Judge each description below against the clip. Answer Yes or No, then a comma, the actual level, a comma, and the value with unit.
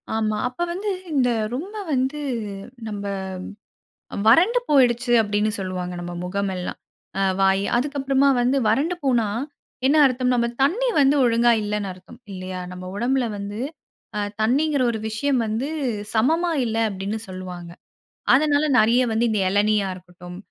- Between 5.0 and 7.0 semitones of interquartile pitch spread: Yes, average, 5.3 semitones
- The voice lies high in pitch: Yes, high, 230 Hz